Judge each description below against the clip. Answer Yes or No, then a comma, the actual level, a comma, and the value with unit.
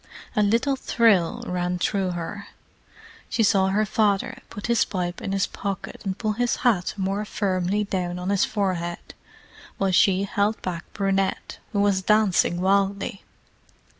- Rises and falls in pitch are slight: Yes, narrow, 2.1 semitones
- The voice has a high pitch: Yes, high, 195 Hz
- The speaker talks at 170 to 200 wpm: No, average, 150 wpm